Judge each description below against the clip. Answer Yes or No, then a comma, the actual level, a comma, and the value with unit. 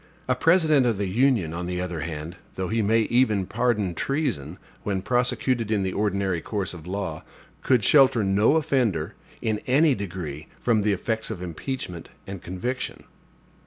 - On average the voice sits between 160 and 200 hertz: No, low, 105 Hz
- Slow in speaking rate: No, average, 160 wpm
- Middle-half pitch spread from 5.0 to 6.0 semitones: Yes, wide, 5.5 semitones